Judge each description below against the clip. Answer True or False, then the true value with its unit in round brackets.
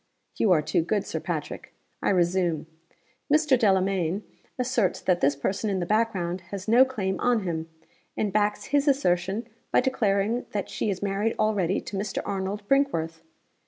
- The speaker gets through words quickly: False (165 wpm)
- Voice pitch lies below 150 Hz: False (200 Hz)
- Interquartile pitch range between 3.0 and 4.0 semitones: True (3.7 semitones)